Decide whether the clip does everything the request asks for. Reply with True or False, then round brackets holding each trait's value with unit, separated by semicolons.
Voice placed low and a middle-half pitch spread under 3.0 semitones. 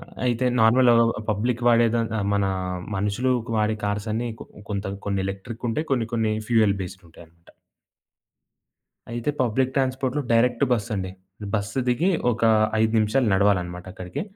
False (110 Hz; 3.3 semitones)